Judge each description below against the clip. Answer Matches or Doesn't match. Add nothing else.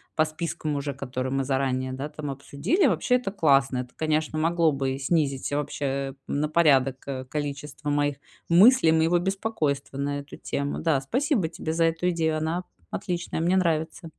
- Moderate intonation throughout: Matches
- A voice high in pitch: Doesn't match